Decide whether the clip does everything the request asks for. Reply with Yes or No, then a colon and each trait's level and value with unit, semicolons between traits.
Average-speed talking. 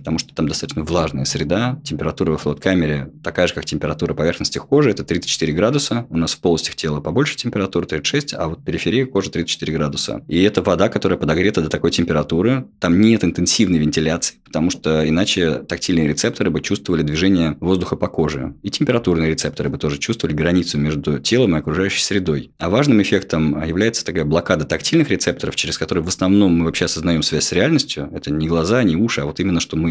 No: fast, 195 wpm